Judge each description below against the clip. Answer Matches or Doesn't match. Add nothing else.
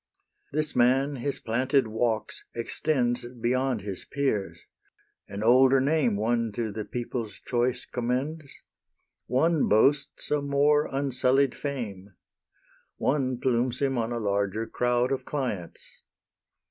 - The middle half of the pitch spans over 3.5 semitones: Doesn't match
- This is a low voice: Matches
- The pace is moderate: Doesn't match